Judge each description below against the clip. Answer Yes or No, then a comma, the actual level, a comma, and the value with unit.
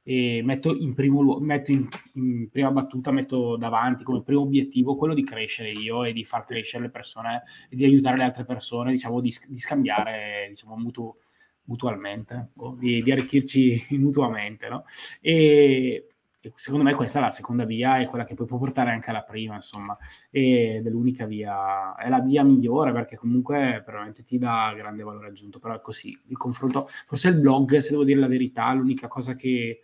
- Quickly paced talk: Yes, fast, 195 wpm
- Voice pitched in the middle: No, low, 125 Hz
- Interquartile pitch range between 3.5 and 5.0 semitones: No, average, 2.9 semitones